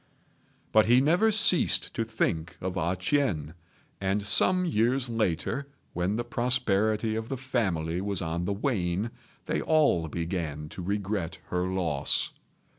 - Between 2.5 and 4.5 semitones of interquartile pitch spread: No, wide, 5.6 semitones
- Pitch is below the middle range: Yes, low, 100 Hz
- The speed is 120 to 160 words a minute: Yes, average, 140 wpm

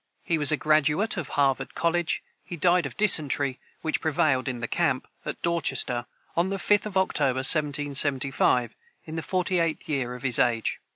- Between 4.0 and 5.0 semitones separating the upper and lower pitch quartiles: Yes, average, 4.3 semitones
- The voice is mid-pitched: Yes, medium, 150 Hz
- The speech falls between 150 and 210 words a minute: Yes, average, 175 wpm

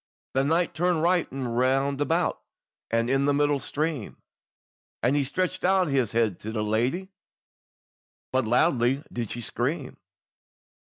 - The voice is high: No, low, 135 Hz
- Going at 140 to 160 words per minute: Yes, average, 145 wpm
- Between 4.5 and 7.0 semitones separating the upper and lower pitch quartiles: Yes, average, 5.0 semitones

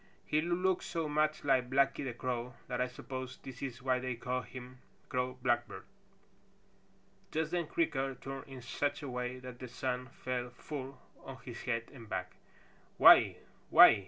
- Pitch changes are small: Yes, narrow, 1.8 semitones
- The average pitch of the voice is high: No, low, 130 Hz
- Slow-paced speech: No, average, 170 wpm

